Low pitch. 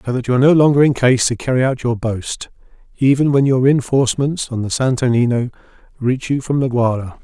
Yes: low, 130 Hz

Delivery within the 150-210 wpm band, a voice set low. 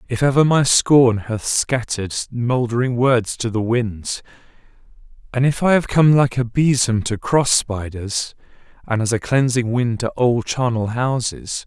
Yes: average, 160 wpm; low, 120 Hz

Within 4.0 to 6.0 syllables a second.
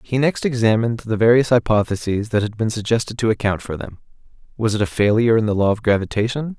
No: 6.4 syllables/s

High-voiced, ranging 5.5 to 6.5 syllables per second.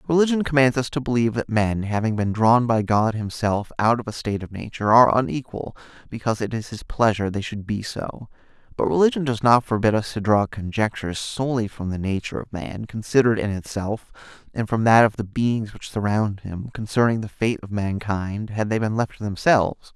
No: low, 110 Hz; 5.7 syllables/s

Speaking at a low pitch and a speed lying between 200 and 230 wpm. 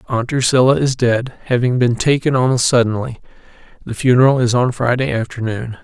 No: low, 125 Hz; average, 155 wpm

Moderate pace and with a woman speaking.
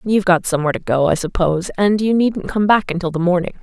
No: fast, 250 wpm; female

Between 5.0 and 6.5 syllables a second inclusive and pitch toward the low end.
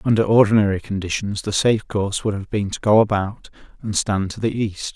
Yes: 5.8 syllables/s; low, 105 Hz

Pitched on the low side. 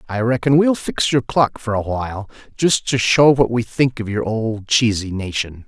Yes: low, 115 Hz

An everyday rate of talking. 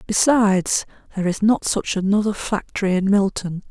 Yes: average, 145 wpm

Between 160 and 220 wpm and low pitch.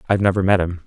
No: fast, 275 wpm; very low, 95 Hz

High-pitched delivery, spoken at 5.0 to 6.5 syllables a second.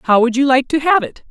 Yes: very high, 260 Hz; 5.7 syllables/s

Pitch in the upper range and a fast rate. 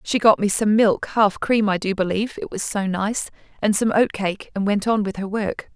Yes: high, 205 Hz; fast, 220 wpm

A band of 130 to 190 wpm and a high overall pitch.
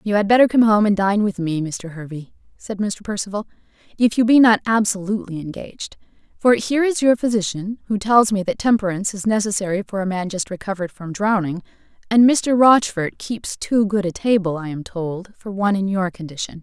No: average, 200 wpm; high, 200 Hz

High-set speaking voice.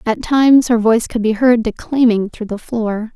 Yes: high, 230 Hz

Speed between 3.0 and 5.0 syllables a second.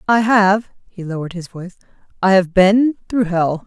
No: 5.4 syllables/s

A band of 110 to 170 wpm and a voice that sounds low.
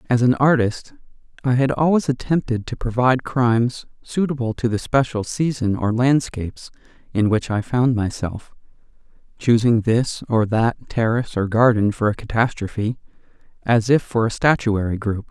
Yes: average, 150 wpm; low, 120 Hz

